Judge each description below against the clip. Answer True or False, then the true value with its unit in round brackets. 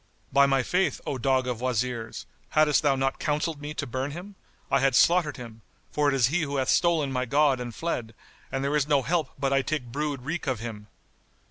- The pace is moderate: False (220 wpm)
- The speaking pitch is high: False (135 Hz)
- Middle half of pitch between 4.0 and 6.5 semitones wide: False (3.0 semitones)